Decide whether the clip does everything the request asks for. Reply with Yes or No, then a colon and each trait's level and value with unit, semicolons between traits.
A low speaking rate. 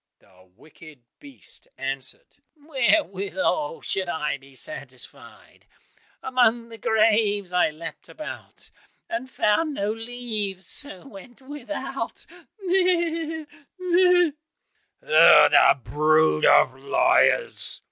Yes: slow, 95 wpm